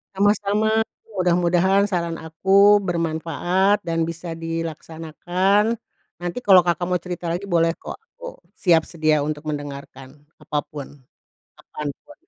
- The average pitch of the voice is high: No, medium, 170 Hz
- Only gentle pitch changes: No, average, 3.2 semitones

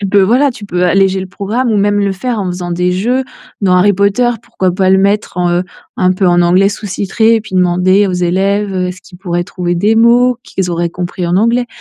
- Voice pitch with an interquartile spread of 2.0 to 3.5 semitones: Yes, narrow, 2.5 semitones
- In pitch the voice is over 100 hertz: Yes, high, 190 Hz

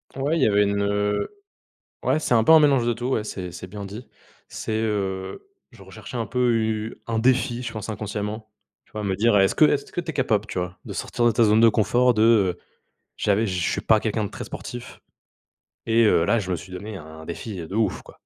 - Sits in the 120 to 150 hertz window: No, low, 110 Hz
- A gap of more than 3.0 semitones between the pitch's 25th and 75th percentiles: No, average, 2.7 semitones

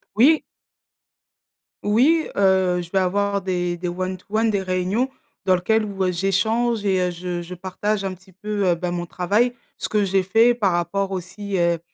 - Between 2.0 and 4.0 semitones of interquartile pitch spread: Yes, narrow, 2.6 semitones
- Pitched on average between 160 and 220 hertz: Yes, high, 190 Hz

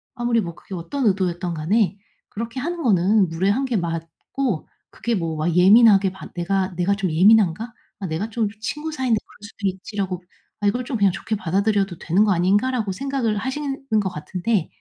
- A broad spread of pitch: No, average, 4.3 semitones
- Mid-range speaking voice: No, high, 200 Hz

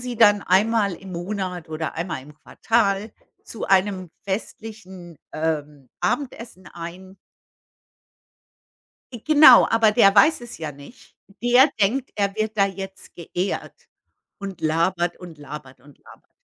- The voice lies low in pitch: No, high, 190 Hz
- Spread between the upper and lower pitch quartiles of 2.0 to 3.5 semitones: No, average, 4.5 semitones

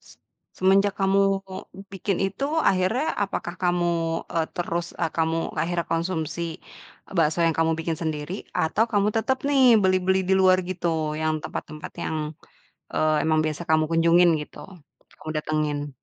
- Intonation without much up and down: No, average, 3.0 semitones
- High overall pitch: No, medium, 170 Hz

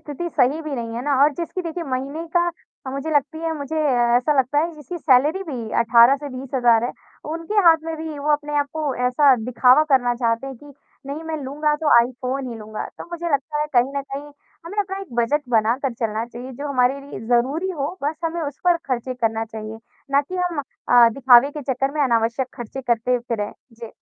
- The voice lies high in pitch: Yes, very high, 275 Hz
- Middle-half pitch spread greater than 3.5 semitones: Yes, average, 3.9 semitones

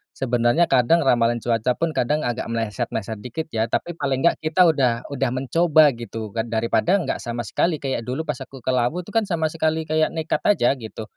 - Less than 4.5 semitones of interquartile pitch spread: No, average, 5.2 semitones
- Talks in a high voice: No, low, 130 Hz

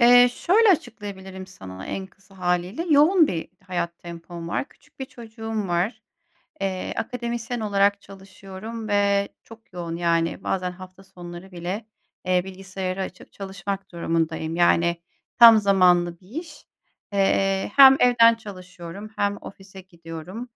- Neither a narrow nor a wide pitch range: Yes, average, 3.7 semitones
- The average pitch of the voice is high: Yes, high, 195 Hz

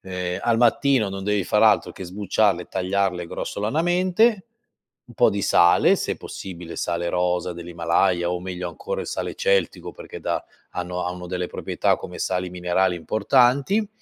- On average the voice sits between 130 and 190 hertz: No, very low, 95 Hz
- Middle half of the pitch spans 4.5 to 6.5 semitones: Yes, wide, 5.4 semitones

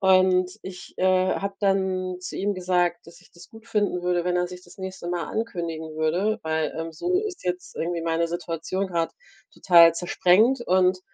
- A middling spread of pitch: No, narrow, 1.9 semitones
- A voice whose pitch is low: No, medium, 180 Hz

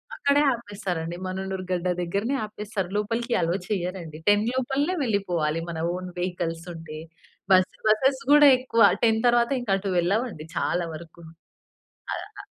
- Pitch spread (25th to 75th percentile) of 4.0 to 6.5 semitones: Yes, average, 5.2 semitones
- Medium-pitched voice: No, high, 195 Hz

